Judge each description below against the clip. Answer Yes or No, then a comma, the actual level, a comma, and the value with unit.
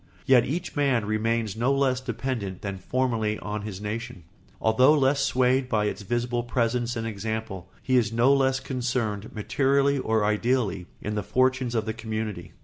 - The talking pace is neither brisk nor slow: Yes, average, 165 wpm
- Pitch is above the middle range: No, low, 115 Hz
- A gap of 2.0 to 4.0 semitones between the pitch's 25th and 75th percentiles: Yes, average, 3.3 semitones